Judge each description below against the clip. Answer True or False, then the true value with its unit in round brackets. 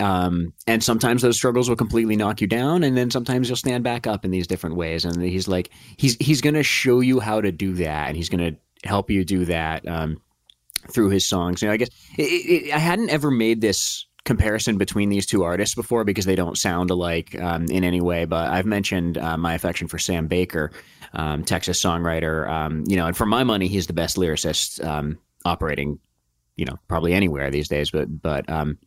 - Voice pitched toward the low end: True (90 Hz)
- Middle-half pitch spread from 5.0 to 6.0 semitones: True (5.3 semitones)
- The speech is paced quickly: True (220 wpm)